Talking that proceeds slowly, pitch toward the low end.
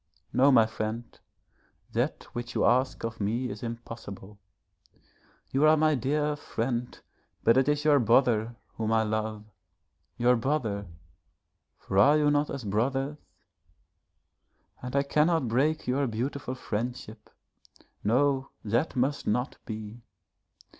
Yes: slow, 125 wpm; low, 125 Hz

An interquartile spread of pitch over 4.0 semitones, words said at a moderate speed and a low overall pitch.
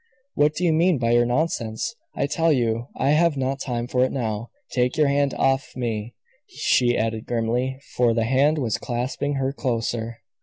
No: average, 3.2 semitones; average, 185 wpm; low, 125 Hz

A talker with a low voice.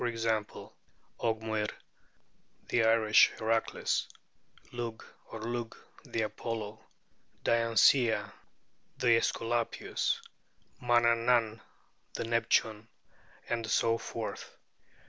Yes: low, 115 Hz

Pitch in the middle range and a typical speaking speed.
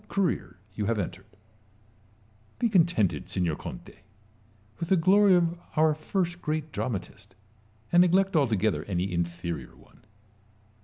No: medium, 155 Hz; slow, 120 wpm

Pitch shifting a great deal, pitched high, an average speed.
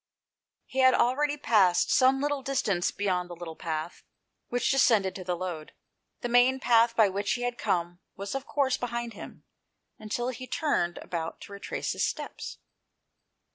Yes: wide, 6.1 semitones; high, 230 Hz; average, 165 wpm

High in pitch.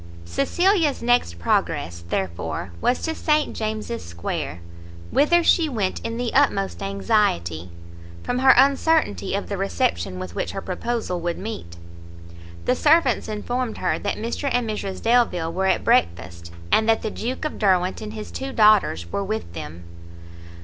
Yes: high, 210 Hz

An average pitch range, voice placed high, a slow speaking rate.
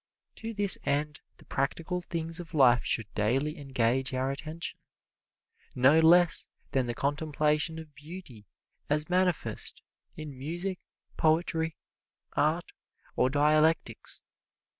No: average, 3.4 semitones; medium, 150 Hz; slow, 115 wpm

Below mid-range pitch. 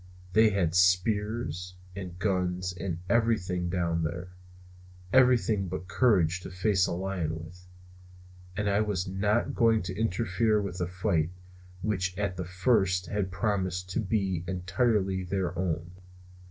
Yes: very low, 95 Hz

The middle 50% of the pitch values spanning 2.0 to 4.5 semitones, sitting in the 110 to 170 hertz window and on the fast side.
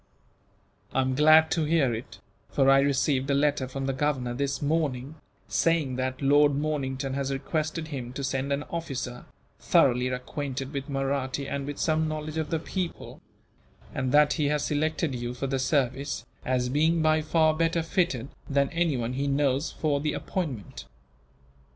No: average, 2.8 semitones; medium, 140 Hz; average, 165 wpm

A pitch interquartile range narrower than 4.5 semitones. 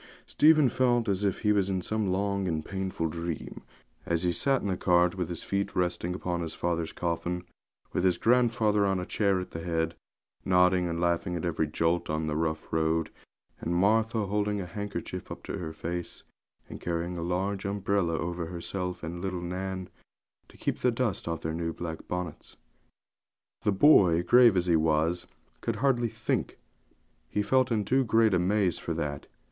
Yes: average, 3.3 semitones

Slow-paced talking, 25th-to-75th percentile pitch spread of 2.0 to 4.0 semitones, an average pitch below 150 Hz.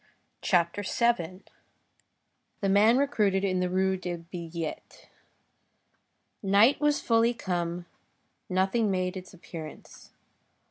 No: slow, 95 wpm; average, 3.4 semitones; high, 190 Hz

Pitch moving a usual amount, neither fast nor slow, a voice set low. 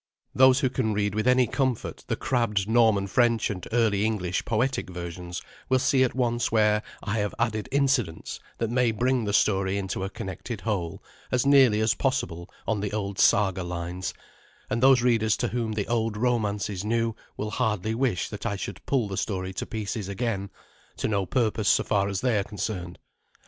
Yes: average, 3.3 semitones; average, 190 wpm; low, 110 Hz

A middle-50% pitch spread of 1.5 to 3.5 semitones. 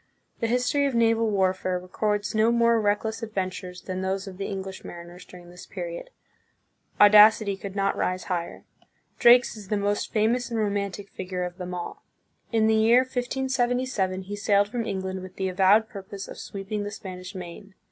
Yes: average, 3.2 semitones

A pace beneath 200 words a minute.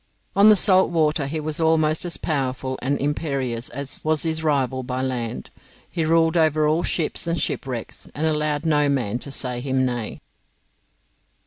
Yes: average, 165 wpm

